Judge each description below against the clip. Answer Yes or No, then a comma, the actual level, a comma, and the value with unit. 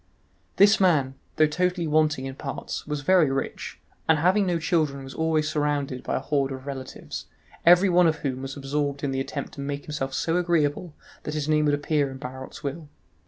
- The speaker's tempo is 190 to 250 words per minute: Yes, average, 200 wpm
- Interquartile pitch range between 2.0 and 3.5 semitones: Yes, average, 2.9 semitones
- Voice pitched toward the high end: No, medium, 150 Hz